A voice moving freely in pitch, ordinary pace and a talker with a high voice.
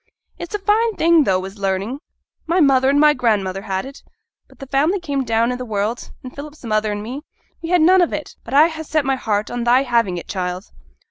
No: wide, 6.3 semitones; fast, 230 wpm; very high, 255 Hz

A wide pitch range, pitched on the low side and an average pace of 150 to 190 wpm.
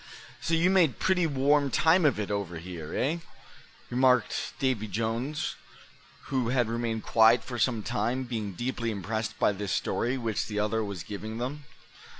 No: average, 3.8 semitones; low, 115 Hz; average, 160 wpm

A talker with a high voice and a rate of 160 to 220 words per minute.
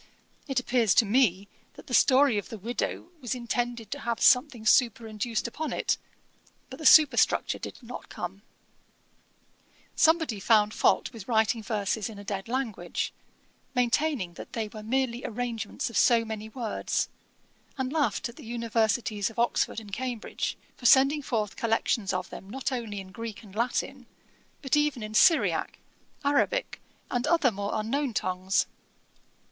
No: high, 230 Hz; average, 150 wpm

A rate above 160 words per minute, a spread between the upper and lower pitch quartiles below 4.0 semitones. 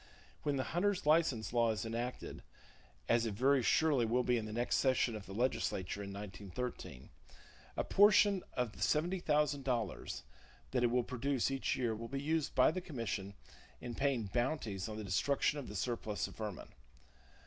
No: average, 170 wpm; average, 4.5 semitones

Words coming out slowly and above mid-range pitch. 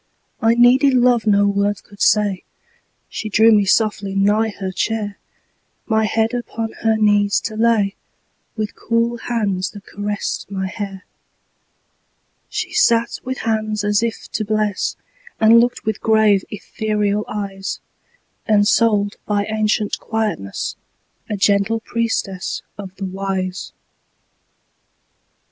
Yes: slow, 120 wpm; high, 210 Hz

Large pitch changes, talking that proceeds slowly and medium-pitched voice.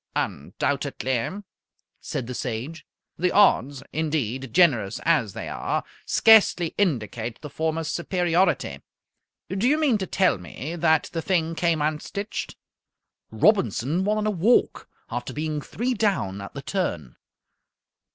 Yes: wide, 6.7 semitones; slow, 130 wpm; medium, 160 Hz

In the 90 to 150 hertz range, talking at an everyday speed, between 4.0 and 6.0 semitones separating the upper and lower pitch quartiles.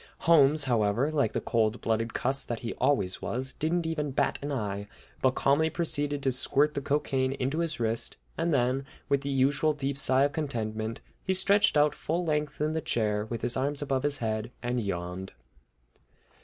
Yes: low, 135 Hz; average, 190 wpm; average, 4.3 semitones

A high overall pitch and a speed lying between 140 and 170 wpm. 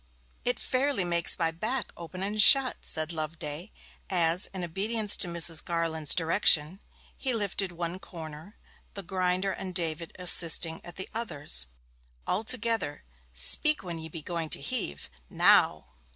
No: medium, 175 Hz; average, 145 wpm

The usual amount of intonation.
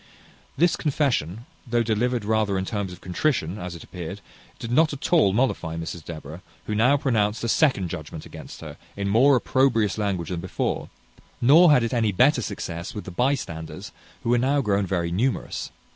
No: wide, 6.0 semitones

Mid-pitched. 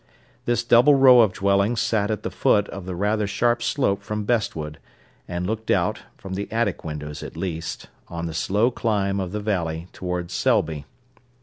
No: low, 100 Hz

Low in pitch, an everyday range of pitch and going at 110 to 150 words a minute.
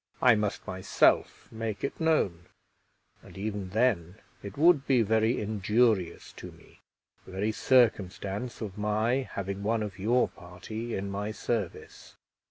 Yes: low, 105 Hz; average, 3.1 semitones; average, 140 wpm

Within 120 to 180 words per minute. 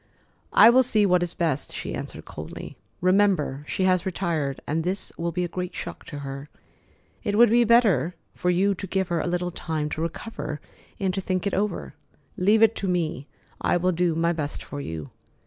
No: average, 200 wpm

